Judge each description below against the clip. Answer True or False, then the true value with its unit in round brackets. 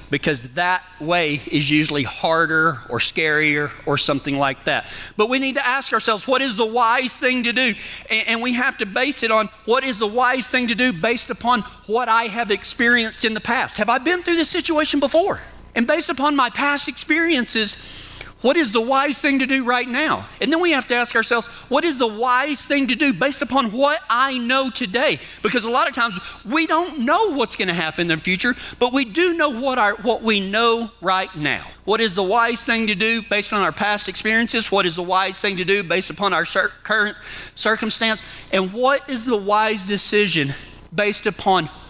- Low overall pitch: False (230 Hz)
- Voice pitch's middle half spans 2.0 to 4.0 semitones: False (4.5 semitones)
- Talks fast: True (210 wpm)